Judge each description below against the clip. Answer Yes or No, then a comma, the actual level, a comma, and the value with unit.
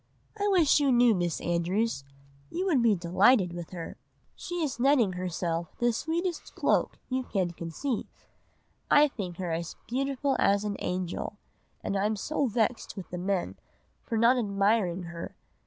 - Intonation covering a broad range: Yes, wide, 6.6 semitones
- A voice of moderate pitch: No, high, 210 Hz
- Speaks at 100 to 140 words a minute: No, average, 160 wpm